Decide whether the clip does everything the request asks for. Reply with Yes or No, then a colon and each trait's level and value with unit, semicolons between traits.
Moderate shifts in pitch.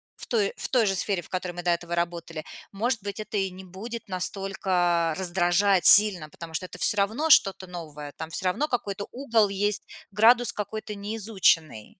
Yes: average, 3.4 semitones